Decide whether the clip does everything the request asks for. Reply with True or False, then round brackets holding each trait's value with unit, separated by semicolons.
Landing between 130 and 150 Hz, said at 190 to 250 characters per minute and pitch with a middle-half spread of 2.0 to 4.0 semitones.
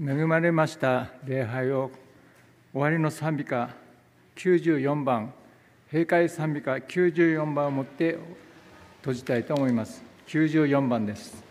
True (140 Hz; 205 characters per minute; 3.7 semitones)